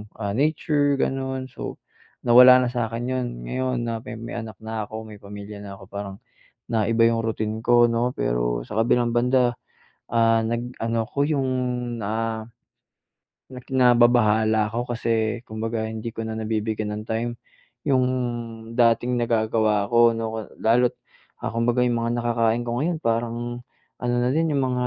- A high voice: No, low, 115 Hz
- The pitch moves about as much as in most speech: No, narrow, 1.9 semitones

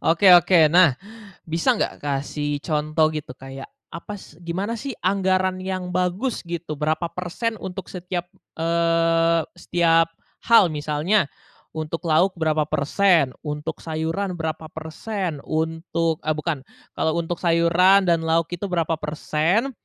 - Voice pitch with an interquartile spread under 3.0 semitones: Yes, narrow, 2.6 semitones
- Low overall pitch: No, medium, 165 Hz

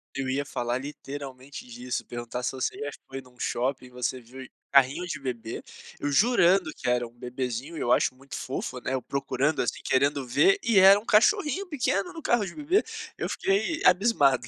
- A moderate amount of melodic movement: No, wide, 7.4 semitones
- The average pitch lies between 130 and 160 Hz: Yes, low, 135 Hz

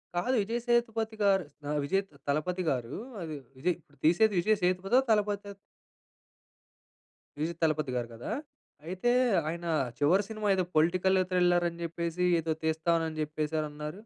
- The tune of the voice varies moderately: Yes, average, 4.2 semitones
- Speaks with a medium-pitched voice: Yes, medium, 175 Hz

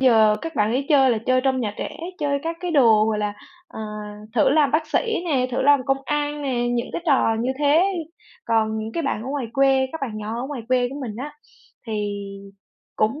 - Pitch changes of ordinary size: Yes, average, 4.4 semitones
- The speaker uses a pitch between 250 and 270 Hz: Yes, very high, 260 Hz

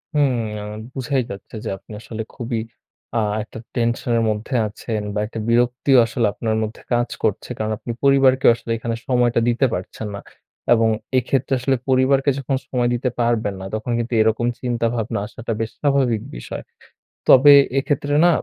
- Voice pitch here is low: Yes, low, 120 Hz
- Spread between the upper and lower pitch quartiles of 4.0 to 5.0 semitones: No, average, 2.7 semitones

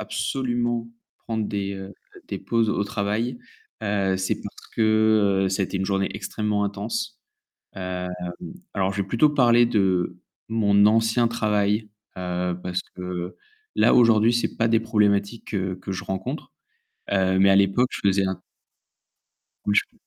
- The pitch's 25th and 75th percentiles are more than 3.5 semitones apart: No, average, 3.0 semitones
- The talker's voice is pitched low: Yes, low, 100 Hz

